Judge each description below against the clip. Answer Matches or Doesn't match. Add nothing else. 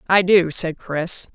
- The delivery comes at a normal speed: Matches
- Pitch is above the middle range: Doesn't match